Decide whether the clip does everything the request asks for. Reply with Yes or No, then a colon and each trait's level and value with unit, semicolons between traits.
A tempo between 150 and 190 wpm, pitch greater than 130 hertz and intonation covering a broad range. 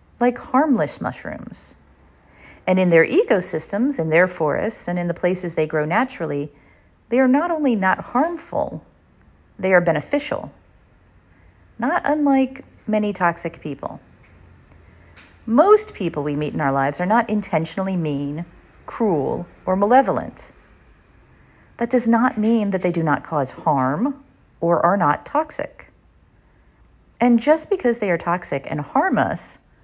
No: slow, 135 wpm; medium, 185 Hz; wide, 8.3 semitones